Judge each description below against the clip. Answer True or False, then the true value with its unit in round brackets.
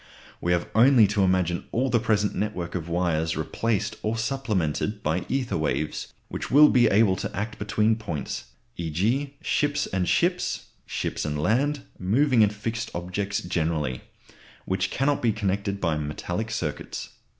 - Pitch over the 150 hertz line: False (105 Hz)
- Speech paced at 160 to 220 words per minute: False (150 wpm)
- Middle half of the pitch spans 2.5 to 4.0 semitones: False (4.9 semitones)